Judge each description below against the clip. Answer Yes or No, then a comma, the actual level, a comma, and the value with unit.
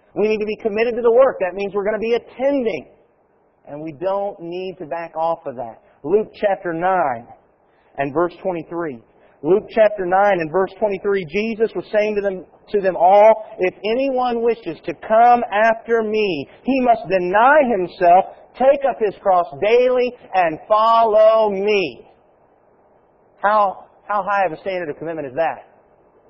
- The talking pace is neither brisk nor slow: Yes, average, 170 wpm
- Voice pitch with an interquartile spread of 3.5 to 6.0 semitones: Yes, average, 3.8 semitones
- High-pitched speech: Yes, high, 205 Hz